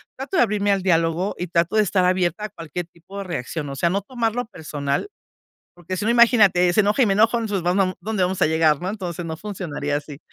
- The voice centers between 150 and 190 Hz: Yes, medium, 185 Hz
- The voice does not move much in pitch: No, average, 4.0 semitones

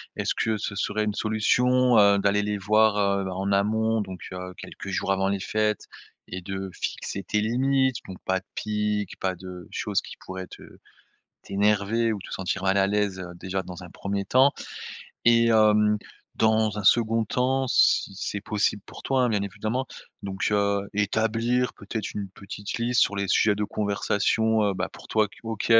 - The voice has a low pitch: Yes, low, 105 Hz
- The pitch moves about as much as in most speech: No, narrow, 2.0 semitones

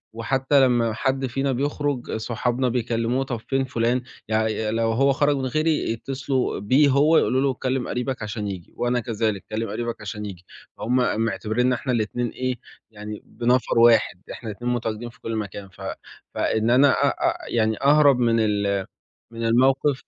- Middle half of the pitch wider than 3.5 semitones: No, average, 3.1 semitones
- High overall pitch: No, low, 120 Hz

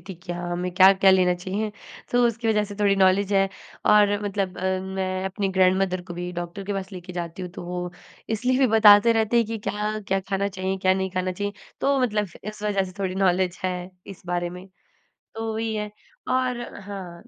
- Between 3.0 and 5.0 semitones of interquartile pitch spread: No, narrow, 2.4 semitones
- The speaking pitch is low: No, high, 195 Hz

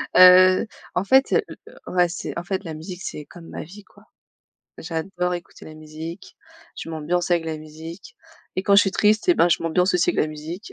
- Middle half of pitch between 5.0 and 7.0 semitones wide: No, narrow, 2.6 semitones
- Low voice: No, medium, 175 Hz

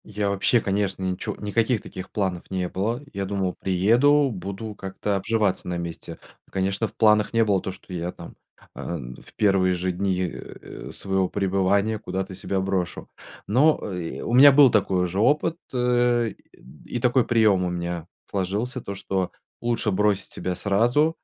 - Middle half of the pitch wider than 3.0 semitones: Yes, average, 3.5 semitones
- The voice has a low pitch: Yes, low, 100 Hz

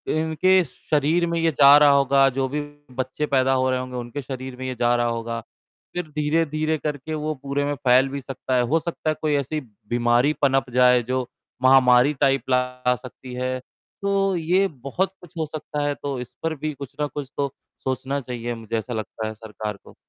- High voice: No, low, 135 Hz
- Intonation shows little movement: No, average, 3.3 semitones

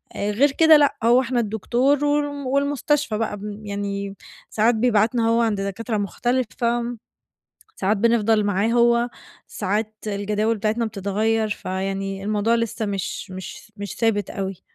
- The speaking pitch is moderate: No, high, 220 Hz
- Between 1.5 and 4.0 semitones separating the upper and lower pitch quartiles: Yes, average, 2.8 semitones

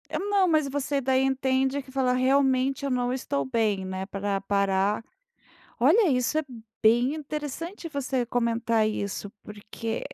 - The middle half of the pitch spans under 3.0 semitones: No, average, 4.5 semitones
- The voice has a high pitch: Yes, very high, 255 Hz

